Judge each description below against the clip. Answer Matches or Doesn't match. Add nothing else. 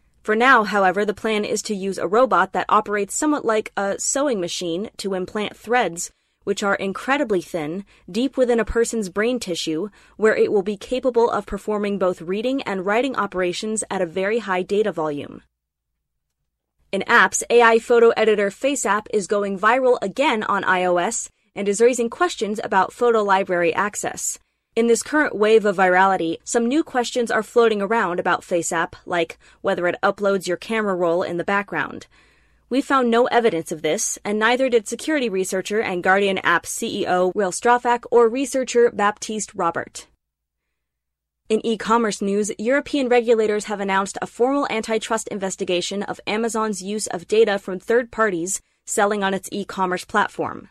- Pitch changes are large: Doesn't match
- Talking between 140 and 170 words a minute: Matches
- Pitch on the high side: Matches